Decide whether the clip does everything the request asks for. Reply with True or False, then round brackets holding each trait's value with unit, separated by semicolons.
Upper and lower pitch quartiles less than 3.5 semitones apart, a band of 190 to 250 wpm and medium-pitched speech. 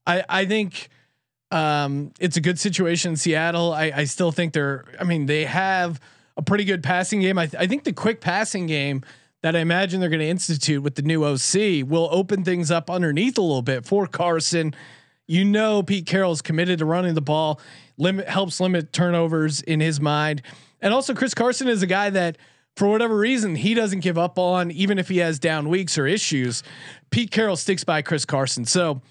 False (3.8 semitones; 205 wpm; 170 Hz)